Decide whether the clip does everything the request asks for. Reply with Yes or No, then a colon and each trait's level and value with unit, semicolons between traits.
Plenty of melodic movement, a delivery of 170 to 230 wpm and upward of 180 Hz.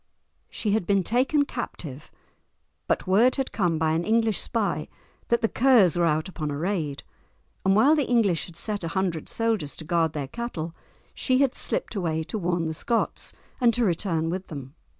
Yes: wide, 6.0 semitones; average, 190 wpm; high, 190 Hz